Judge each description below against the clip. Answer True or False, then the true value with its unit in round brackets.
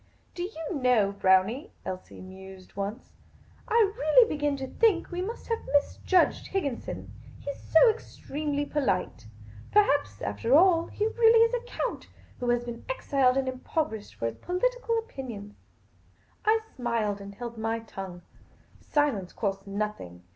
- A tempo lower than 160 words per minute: True (150 wpm)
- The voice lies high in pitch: True (265 Hz)